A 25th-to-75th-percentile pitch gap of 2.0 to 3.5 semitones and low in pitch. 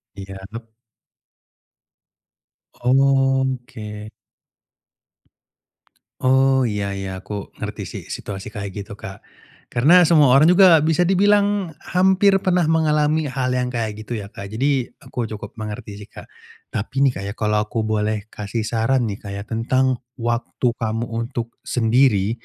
No: average, 4.5 semitones; low, 120 Hz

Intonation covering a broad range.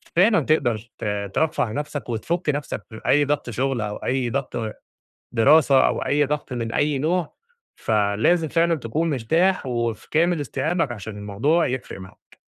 Yes: wide, 5.7 semitones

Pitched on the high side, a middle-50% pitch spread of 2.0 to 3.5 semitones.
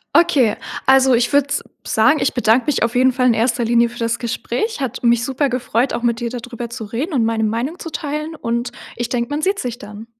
Yes: high, 240 Hz; average, 2.7 semitones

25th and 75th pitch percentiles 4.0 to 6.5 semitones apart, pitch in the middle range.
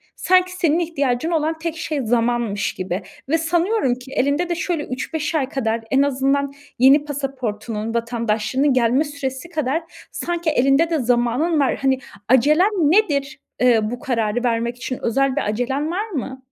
No: average, 4.7 semitones; very high, 275 Hz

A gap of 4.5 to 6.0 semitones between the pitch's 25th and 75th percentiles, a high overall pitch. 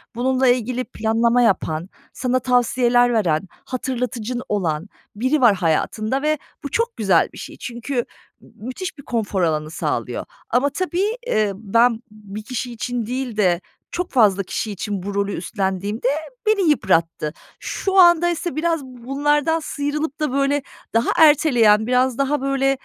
Yes: average, 5.1 semitones; high, 245 Hz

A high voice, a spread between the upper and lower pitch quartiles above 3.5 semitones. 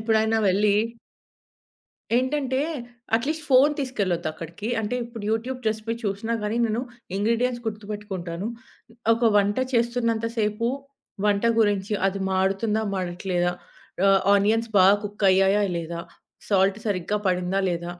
No: high, 210 Hz; average, 3.1 semitones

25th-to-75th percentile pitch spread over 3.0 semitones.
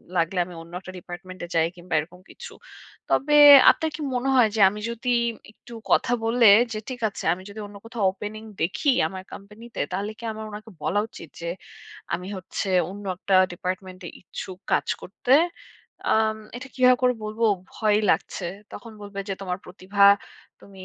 Yes: average, 3.6 semitones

